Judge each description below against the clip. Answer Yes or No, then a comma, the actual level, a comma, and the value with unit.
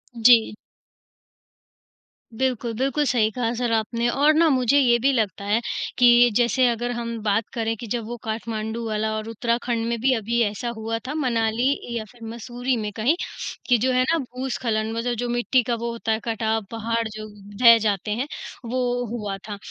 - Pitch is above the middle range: Yes, high, 235 Hz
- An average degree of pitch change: No, narrow, 1.9 semitones